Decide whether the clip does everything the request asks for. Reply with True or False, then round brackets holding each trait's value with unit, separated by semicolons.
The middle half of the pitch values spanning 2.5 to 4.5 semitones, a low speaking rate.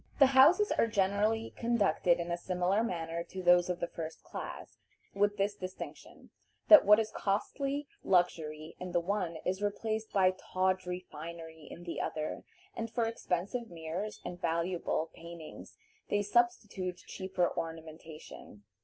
False (3.8 semitones; 145 wpm)